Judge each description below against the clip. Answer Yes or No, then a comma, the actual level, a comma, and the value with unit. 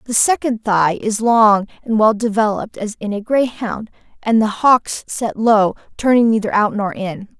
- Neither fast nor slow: Yes, average, 180 wpm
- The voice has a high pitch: Yes, high, 210 Hz